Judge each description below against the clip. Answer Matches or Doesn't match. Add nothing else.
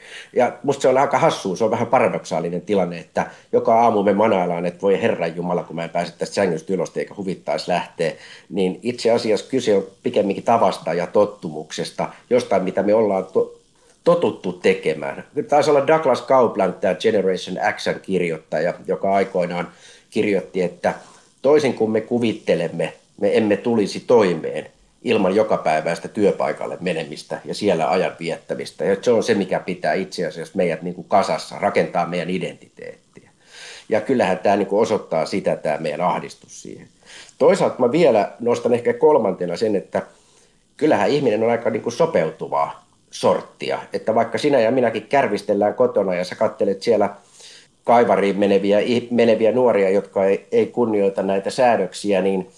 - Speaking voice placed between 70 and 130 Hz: Doesn't match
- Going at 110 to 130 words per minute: Doesn't match